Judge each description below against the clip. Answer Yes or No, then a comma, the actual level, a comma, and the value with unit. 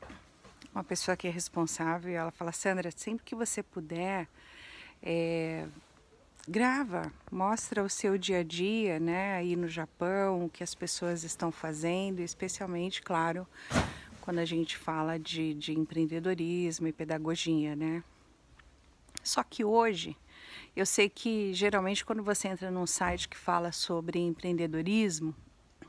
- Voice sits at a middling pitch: Yes, medium, 175 Hz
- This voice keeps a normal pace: Yes, average, 135 wpm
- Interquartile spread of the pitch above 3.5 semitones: No, average, 2.8 semitones